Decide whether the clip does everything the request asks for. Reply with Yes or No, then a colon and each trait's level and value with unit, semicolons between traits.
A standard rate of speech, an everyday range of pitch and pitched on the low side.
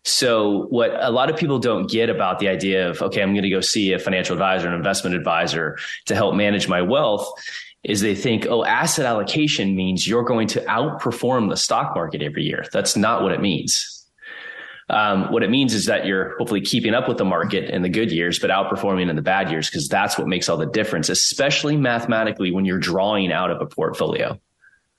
No: fast, 215 wpm; average, 4.4 semitones; low, 100 Hz